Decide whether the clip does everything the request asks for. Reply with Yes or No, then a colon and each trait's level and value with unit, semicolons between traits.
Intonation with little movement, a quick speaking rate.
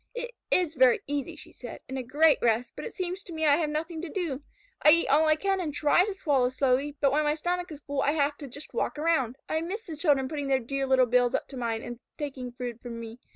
No: average, 3.9 semitones; fast, 265 wpm